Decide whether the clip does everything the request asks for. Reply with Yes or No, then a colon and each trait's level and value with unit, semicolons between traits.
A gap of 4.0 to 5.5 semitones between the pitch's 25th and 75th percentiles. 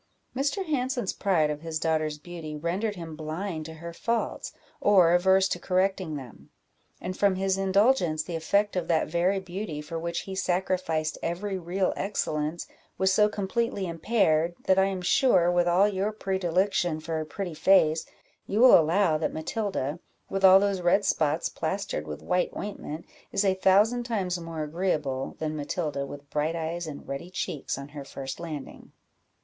No: average, 3.6 semitones